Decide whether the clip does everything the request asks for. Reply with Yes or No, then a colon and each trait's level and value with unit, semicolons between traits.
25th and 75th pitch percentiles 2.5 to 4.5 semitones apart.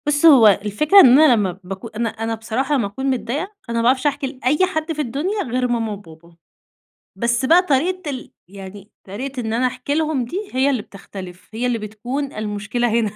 No: average, 4.9 semitones